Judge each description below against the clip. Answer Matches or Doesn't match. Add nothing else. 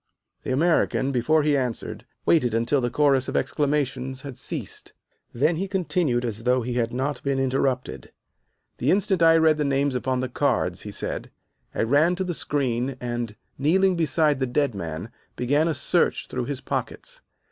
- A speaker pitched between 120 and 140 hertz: Matches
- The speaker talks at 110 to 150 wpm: Doesn't match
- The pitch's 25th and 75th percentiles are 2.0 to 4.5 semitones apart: Matches